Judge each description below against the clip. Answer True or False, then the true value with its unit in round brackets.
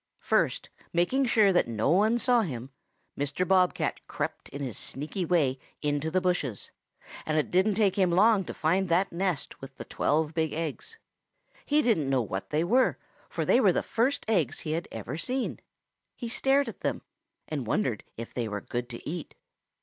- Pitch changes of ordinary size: False (6.3 semitones)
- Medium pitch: True (170 Hz)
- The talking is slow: False (190 wpm)